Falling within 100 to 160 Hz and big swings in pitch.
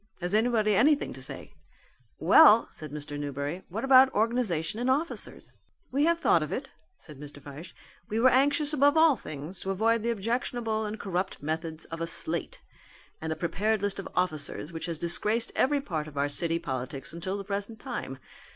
No: high, 195 Hz; wide, 6.8 semitones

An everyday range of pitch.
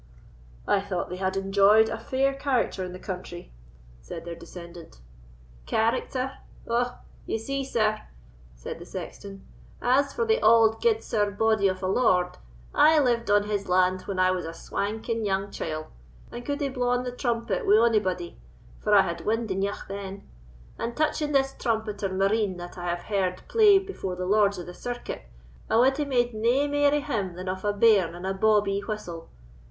Yes: average, 4.6 semitones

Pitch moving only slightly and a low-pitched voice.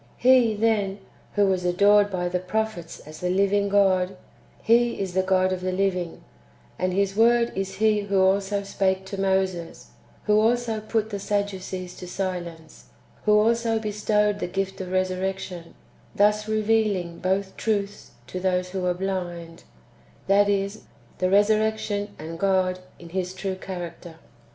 No: narrow, 2.3 semitones; high, 195 Hz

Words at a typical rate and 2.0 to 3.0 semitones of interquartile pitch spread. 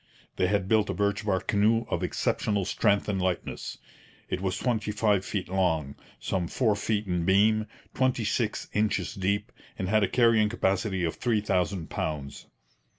Yes: average, 165 wpm; narrow, 2.6 semitones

